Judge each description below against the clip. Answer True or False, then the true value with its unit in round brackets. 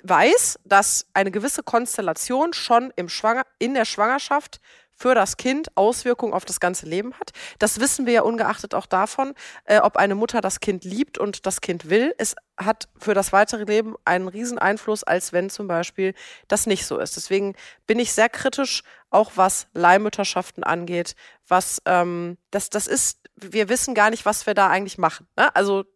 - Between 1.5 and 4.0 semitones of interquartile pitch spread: True (3.6 semitones)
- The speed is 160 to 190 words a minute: True (185 wpm)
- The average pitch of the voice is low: False (210 Hz)